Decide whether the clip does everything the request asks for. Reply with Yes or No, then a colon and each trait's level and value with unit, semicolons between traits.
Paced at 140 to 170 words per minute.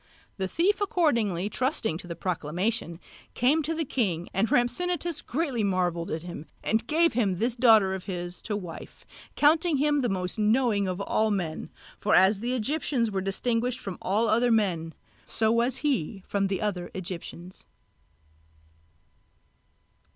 Yes: average, 160 wpm